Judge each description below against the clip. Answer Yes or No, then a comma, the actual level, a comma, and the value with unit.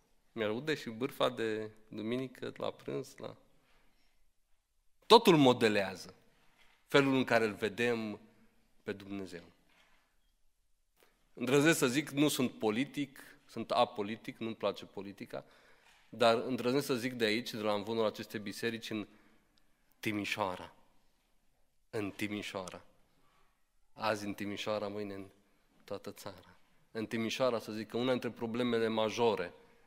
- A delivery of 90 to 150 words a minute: Yes, average, 120 wpm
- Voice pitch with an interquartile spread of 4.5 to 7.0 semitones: No, average, 3.0 semitones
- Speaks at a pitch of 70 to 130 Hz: Yes, low, 110 Hz